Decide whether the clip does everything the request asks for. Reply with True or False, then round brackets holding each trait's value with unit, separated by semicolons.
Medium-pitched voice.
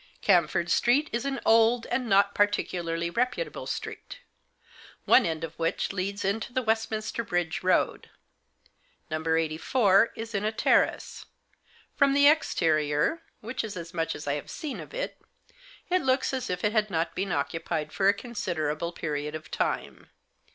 False (200 Hz)